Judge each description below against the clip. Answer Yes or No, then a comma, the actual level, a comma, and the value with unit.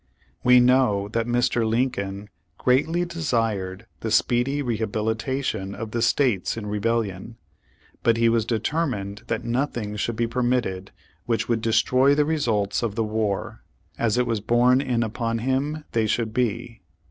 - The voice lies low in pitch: Yes, low, 115 Hz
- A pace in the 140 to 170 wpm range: Yes, average, 145 wpm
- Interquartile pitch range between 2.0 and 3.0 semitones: Yes, average, 2.7 semitones